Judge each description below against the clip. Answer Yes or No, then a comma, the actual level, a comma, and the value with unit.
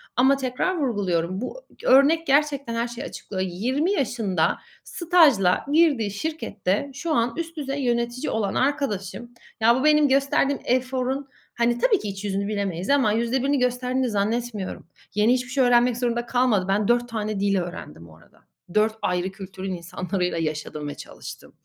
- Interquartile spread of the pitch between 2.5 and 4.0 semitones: No, wide, 5.5 semitones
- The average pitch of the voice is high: Yes, high, 240 Hz